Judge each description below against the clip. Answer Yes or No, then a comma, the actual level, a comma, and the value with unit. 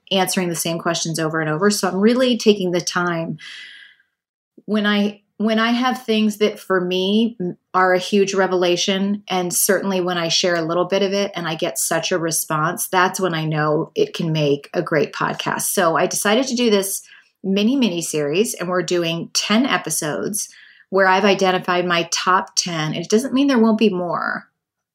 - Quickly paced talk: No, average, 190 wpm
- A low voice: No, medium, 185 Hz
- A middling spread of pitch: Yes, average, 3.5 semitones